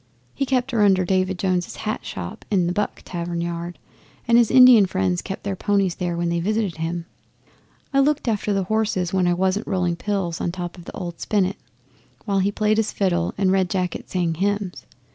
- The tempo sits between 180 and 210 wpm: Yes, average, 200 wpm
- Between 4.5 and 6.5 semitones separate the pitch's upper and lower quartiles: No, average, 3.1 semitones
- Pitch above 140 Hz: Yes, high, 190 Hz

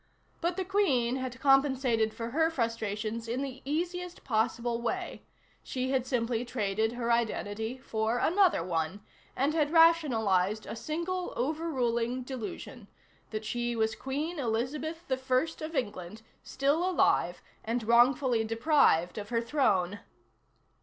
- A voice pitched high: Yes, high, 245 Hz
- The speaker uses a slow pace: Yes, slow, 130 wpm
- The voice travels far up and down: No, average, 4.7 semitones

